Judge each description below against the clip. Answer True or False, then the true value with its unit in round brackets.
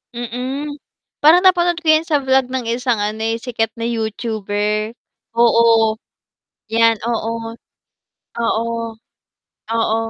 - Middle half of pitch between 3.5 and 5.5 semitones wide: False (2.8 semitones)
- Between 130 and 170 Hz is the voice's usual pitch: False (230 Hz)